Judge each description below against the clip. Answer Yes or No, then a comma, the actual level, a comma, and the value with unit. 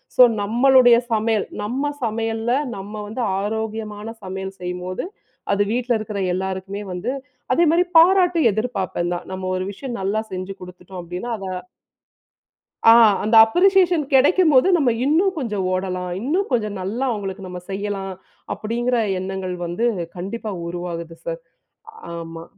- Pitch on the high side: Yes, high, 210 Hz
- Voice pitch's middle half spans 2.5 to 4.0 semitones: No, average, 4.7 semitones